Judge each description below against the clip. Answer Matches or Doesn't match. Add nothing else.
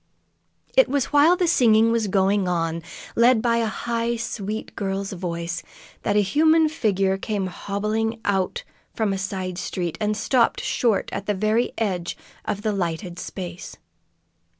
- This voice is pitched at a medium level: Doesn't match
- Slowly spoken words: Doesn't match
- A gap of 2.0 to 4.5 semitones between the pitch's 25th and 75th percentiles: Matches